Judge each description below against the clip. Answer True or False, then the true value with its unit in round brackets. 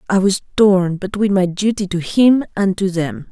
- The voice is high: True (195 Hz)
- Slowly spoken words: False (200 wpm)